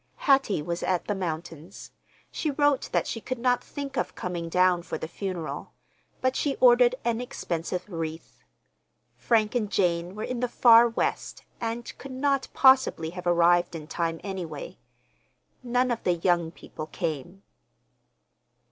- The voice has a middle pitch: No, high, 195 Hz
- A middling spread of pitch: No, wide, 6.5 semitones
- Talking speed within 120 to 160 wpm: Yes, average, 150 wpm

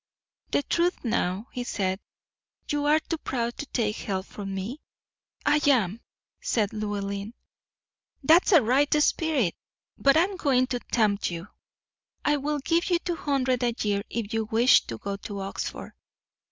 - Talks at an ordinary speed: Yes, average, 160 wpm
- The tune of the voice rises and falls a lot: Yes, wide, 6.3 semitones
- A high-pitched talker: Yes, high, 240 Hz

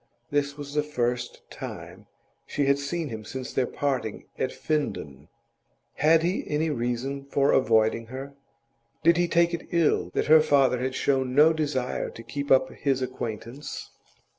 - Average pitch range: Yes, average, 3.1 semitones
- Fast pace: No, average, 160 wpm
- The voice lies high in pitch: No, medium, 140 Hz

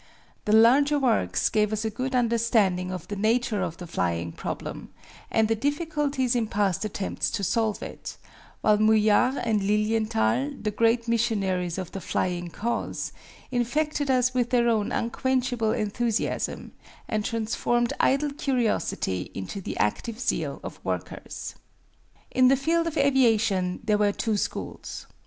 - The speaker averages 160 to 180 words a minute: No, average, 145 wpm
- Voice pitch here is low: No, high, 225 Hz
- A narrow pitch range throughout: No, average, 3.6 semitones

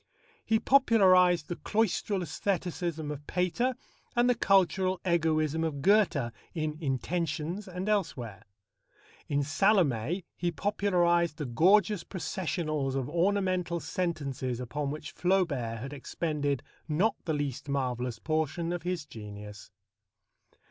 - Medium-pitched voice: Yes, medium, 165 Hz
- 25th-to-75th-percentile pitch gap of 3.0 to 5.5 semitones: Yes, average, 4.6 semitones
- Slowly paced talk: Yes, slow, 115 wpm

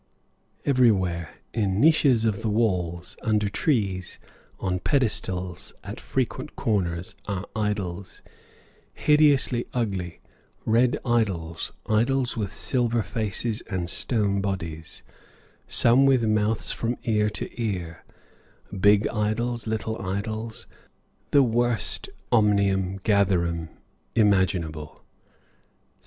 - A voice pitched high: No, low, 105 Hz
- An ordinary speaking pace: No, slow, 95 wpm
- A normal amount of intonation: Yes, average, 4.0 semitones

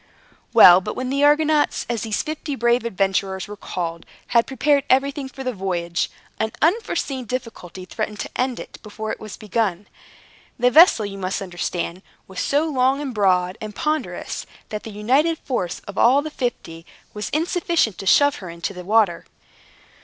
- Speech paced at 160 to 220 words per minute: Yes, average, 170 wpm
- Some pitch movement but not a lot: No, wide, 6.3 semitones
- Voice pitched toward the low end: No, high, 225 Hz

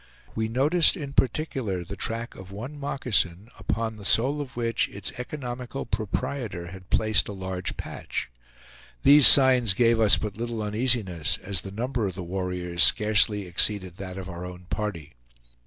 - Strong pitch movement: No, average, 4.8 semitones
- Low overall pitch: Yes, low, 105 Hz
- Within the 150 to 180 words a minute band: Yes, average, 160 wpm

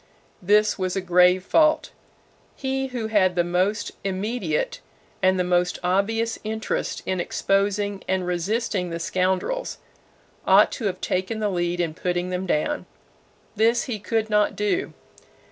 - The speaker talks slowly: No, average, 145 wpm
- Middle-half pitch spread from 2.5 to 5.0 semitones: Yes, average, 3.4 semitones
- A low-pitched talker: No, high, 195 Hz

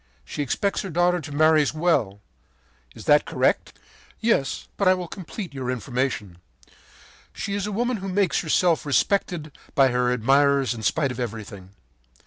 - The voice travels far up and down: Yes, wide, 6.5 semitones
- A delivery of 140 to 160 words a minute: Yes, average, 155 wpm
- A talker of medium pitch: Yes, medium, 145 Hz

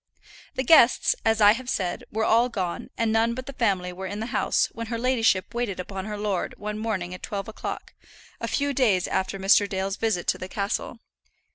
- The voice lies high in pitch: Yes, high, 210 Hz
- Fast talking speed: Yes, fast, 210 wpm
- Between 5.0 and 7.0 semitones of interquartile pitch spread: No, average, 3.3 semitones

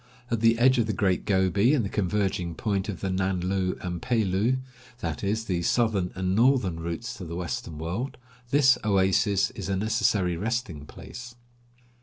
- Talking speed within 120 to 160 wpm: No, average, 190 wpm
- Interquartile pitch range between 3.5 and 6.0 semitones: Yes, average, 4.2 semitones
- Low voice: Yes, low, 100 Hz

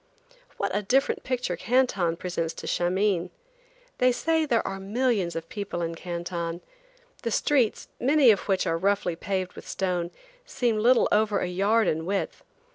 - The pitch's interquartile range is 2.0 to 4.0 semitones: No, average, 5.3 semitones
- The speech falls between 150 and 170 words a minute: Yes, average, 160 wpm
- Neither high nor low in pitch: No, high, 200 Hz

